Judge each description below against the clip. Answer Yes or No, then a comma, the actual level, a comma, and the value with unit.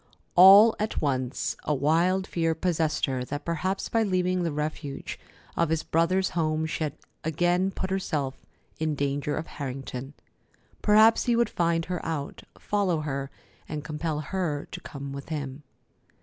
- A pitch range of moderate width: Yes, average, 4.1 semitones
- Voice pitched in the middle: Yes, medium, 160 Hz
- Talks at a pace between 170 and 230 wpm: No, average, 155 wpm